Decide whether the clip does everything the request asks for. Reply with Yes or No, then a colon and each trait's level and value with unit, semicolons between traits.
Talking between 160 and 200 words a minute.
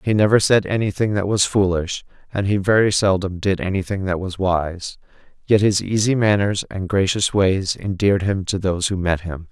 Yes: average, 190 wpm